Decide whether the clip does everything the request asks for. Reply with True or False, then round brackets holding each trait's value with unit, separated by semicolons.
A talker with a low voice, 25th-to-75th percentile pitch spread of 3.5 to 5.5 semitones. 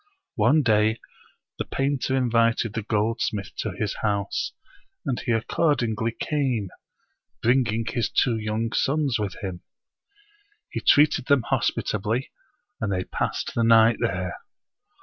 False (115 Hz; 3.1 semitones)